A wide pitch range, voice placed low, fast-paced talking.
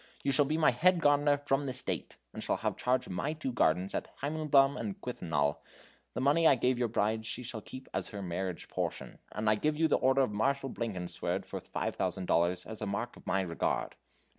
Yes: wide, 6.3 semitones; low, 125 Hz; fast, 215 wpm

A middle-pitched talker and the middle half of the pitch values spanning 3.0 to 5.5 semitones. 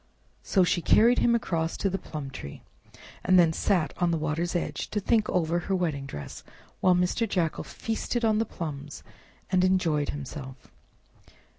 Yes: medium, 175 Hz; average, 3.9 semitones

